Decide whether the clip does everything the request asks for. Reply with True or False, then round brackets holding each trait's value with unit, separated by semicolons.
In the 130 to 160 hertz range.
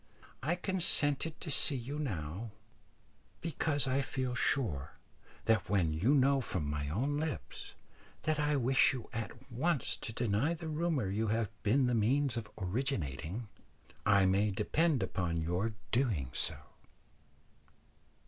False (120 Hz)